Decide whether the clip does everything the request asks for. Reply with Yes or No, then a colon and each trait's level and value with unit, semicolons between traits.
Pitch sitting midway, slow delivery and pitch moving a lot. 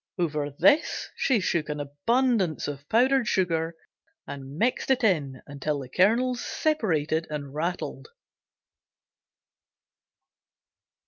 Yes: medium, 165 Hz; slow, 105 wpm; wide, 8.2 semitones